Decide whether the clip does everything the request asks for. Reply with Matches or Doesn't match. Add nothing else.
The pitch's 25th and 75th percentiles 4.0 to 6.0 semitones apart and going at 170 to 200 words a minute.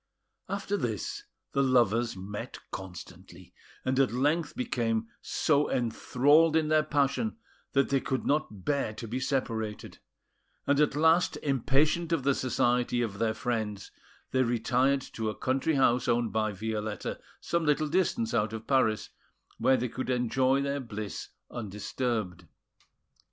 Doesn't match